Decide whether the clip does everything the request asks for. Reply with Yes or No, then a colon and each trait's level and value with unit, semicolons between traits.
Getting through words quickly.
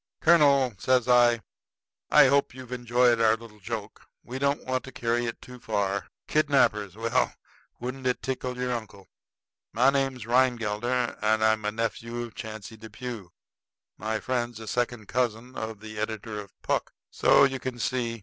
No: average, 160 wpm